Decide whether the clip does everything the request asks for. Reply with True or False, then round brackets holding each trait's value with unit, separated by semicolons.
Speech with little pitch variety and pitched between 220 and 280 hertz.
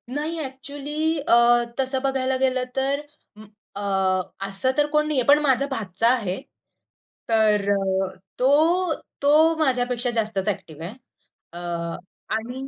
False (4.5 semitones; 260 Hz)